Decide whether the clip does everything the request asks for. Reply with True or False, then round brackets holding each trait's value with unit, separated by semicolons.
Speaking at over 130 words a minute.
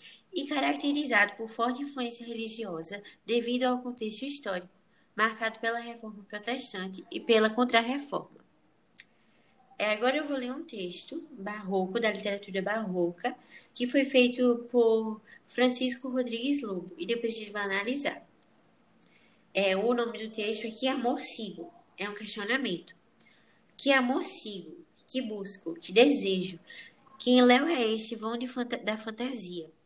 True (140 wpm)